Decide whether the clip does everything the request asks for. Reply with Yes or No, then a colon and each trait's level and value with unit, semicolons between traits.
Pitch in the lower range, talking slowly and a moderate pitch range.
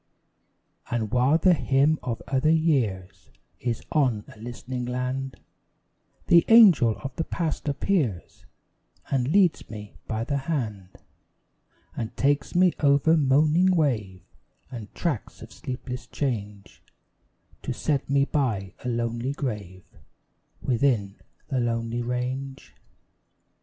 Yes: low, 130 Hz; slow, 115 wpm; average, 4.0 semitones